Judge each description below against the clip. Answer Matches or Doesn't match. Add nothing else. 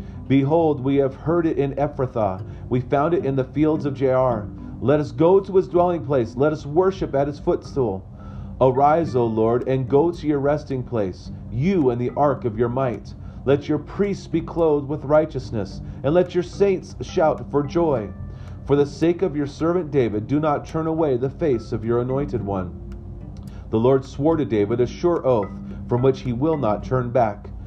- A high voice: Doesn't match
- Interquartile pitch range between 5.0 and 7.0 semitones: Matches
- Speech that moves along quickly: Doesn't match